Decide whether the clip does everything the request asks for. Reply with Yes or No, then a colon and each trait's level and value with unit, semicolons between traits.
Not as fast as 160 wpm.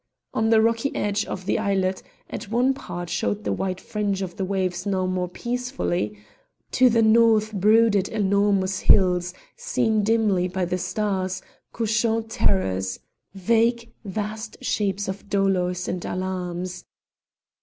Yes: slow, 135 wpm